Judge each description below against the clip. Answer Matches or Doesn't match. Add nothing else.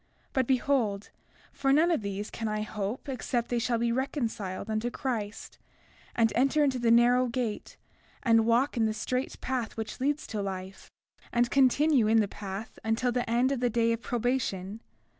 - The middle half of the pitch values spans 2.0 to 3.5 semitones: Matches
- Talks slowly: Doesn't match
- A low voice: Doesn't match